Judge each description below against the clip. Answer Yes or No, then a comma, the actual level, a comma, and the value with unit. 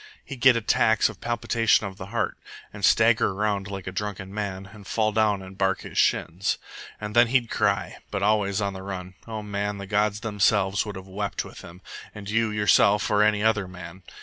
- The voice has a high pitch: No, low, 105 Hz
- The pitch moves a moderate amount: No, narrow, 1.9 semitones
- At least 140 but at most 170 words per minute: No, average, 200 wpm